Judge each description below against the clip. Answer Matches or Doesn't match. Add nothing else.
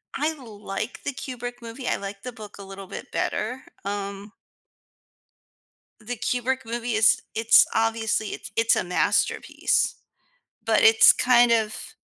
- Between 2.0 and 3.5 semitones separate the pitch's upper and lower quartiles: Matches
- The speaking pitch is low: Doesn't match